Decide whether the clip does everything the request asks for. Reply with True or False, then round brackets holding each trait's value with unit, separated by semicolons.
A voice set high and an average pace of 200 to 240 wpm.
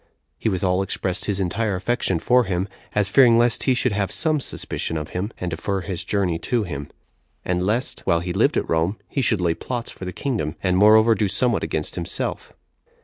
False (100 Hz; 205 wpm)